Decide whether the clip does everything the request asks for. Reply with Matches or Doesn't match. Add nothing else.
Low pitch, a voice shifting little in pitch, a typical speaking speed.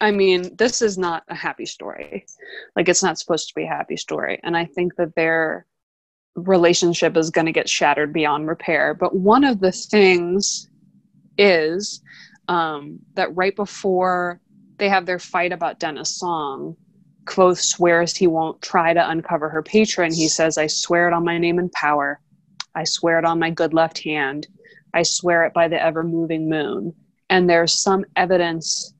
Doesn't match